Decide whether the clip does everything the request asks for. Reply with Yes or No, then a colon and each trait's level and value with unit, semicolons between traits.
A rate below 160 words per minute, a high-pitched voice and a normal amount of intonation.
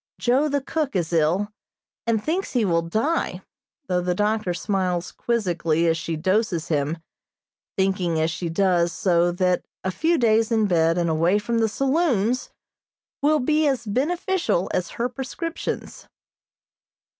No: average, 145 wpm; high, 200 Hz; wide, 6.5 semitones